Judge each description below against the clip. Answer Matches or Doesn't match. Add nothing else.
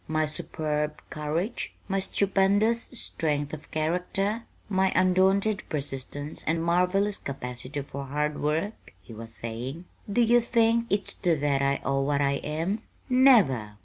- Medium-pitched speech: Matches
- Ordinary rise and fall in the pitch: Doesn't match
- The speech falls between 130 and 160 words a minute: Matches